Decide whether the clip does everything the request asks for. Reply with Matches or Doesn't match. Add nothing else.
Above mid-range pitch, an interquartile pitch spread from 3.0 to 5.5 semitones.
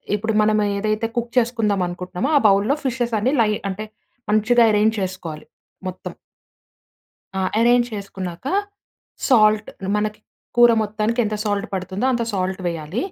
Matches